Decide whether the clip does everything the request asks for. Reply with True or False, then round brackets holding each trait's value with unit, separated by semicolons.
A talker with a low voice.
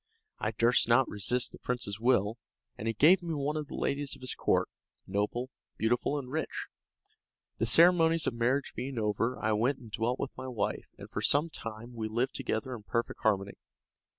True (120 Hz)